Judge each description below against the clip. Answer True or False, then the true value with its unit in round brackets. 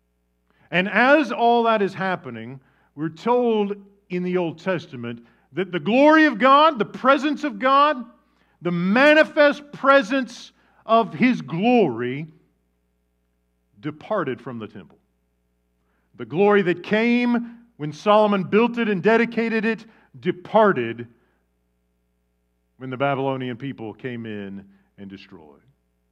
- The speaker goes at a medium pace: False (115 wpm)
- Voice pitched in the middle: True (175 Hz)